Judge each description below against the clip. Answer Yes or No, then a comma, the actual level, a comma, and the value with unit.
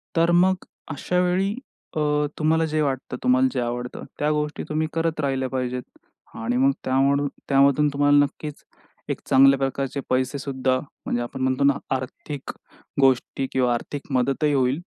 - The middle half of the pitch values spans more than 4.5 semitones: No, average, 2.7 semitones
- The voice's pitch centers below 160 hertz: Yes, medium, 140 Hz